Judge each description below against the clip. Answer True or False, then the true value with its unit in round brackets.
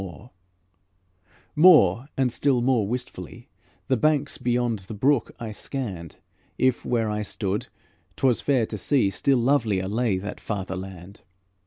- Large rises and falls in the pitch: False (4.7 semitones)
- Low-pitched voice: True (115 Hz)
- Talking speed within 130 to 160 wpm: True (140 wpm)